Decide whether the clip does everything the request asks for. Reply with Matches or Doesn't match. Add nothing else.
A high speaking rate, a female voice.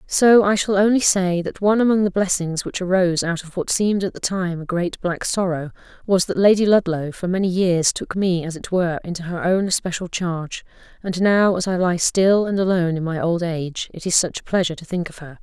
Matches